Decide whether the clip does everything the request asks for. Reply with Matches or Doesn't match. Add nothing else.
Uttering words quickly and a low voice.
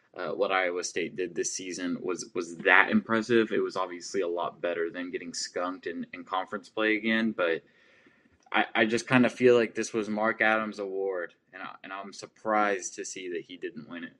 Matches